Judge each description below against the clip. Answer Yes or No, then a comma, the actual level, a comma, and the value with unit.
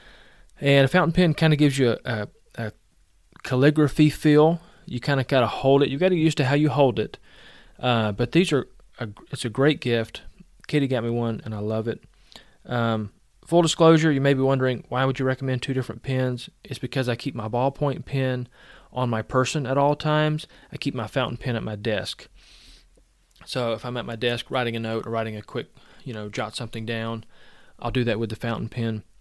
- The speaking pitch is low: Yes, low, 125 Hz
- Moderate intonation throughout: Yes, average, 3.7 semitones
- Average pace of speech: No, fast, 215 wpm